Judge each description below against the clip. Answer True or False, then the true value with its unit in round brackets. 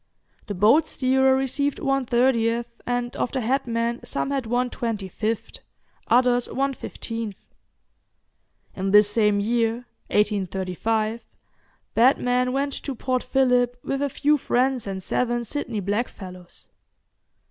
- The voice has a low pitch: False (240 Hz)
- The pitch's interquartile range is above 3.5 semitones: False (3.2 semitones)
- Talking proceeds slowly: True (125 wpm)